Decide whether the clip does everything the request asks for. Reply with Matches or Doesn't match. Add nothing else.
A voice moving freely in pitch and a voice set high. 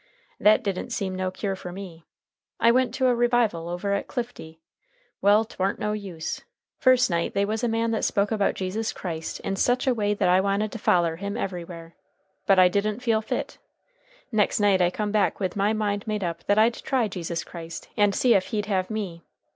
Doesn't match